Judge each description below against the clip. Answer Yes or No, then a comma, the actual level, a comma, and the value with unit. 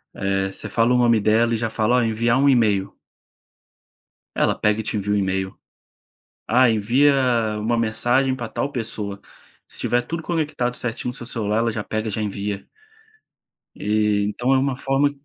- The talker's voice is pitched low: Yes, low, 115 Hz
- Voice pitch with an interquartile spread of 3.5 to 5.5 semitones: No, average, 2.9 semitones